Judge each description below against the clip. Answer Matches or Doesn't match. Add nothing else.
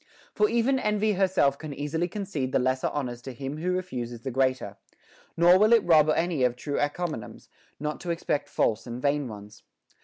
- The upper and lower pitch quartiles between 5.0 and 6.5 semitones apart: Matches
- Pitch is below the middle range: Doesn't match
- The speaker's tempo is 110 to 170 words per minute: Doesn't match